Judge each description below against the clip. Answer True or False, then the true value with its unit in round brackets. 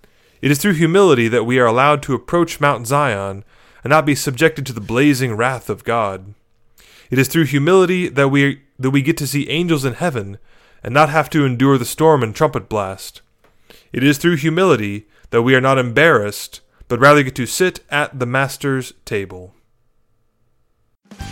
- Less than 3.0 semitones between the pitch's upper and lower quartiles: False (4.2 semitones)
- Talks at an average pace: True (180 wpm)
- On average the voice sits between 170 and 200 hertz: False (135 Hz)